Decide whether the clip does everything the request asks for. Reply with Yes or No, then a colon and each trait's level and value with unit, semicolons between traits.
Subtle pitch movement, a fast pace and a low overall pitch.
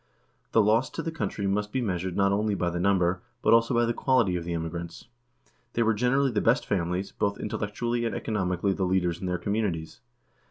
No: average, 4.3 semitones; fast, 210 wpm; low, 100 Hz